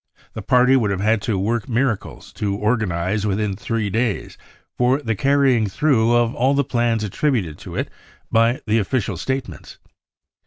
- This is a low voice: Yes, low, 115 Hz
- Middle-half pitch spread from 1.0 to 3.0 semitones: No, average, 3.6 semitones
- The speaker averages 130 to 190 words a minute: Yes, average, 160 wpm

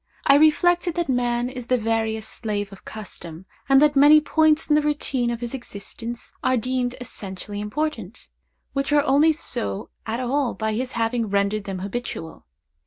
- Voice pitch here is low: No, high, 245 Hz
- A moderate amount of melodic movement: Yes, average, 4.8 semitones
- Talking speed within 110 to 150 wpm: No, average, 170 wpm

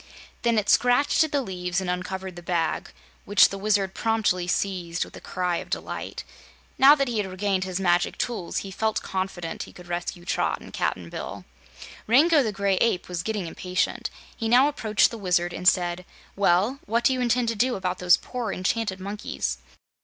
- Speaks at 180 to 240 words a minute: Yes, average, 190 wpm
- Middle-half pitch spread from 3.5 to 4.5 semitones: Yes, average, 4.1 semitones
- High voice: Yes, high, 195 Hz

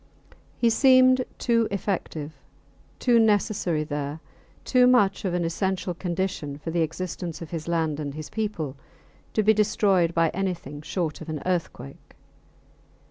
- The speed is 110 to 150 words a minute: Yes, average, 140 wpm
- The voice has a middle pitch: Yes, medium, 180 Hz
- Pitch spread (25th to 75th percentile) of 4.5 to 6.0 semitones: Yes, average, 5.1 semitones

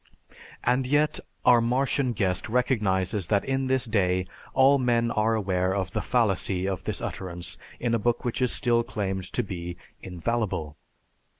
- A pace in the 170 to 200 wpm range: No, average, 160 wpm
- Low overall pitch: Yes, low, 110 Hz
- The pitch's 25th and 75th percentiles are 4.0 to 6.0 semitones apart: Yes, average, 4.7 semitones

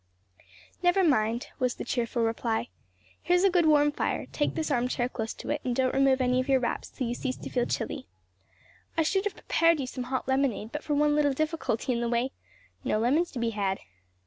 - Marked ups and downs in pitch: No, average, 3.9 semitones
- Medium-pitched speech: No, very high, 260 Hz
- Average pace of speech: No, fast, 220 wpm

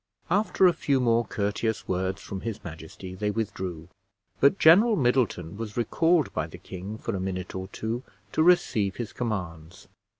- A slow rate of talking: No, average, 165 wpm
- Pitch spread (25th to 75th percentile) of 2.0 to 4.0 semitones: No, average, 5.1 semitones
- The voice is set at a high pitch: No, low, 105 Hz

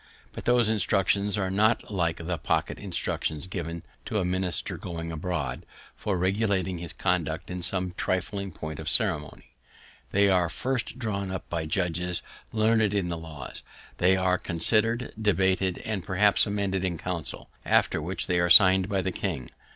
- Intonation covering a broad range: No, average, 2.8 semitones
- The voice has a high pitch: No, very low, 95 Hz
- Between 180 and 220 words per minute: No, average, 165 wpm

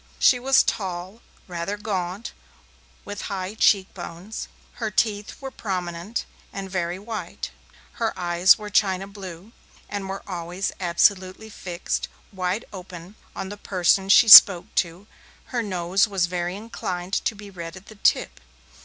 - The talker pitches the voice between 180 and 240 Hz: Yes, high, 190 Hz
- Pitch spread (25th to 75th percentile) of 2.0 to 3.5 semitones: Yes, narrow, 2.6 semitones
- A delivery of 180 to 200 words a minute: No, average, 140 wpm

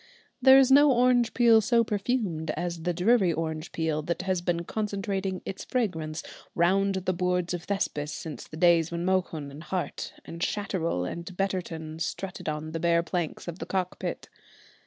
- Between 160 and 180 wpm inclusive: Yes, average, 170 wpm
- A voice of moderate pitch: Yes, medium, 180 Hz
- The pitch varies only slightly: No, average, 3.2 semitones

